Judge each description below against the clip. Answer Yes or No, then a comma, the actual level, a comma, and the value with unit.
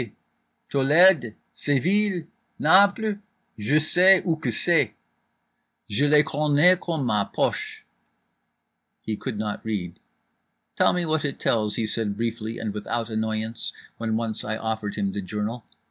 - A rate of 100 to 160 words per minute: Yes, average, 140 wpm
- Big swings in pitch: Yes, wide, 6.4 semitones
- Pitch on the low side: Yes, low, 115 Hz